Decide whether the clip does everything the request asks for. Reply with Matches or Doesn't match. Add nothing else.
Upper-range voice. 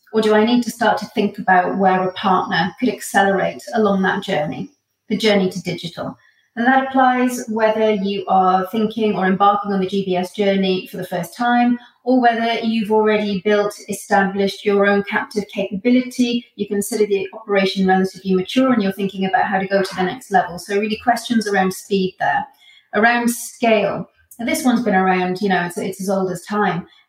Matches